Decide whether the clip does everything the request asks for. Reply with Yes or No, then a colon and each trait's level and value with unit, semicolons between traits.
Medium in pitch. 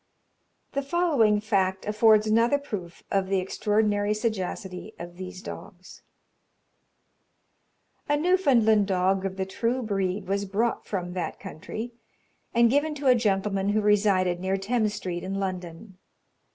No: high, 205 Hz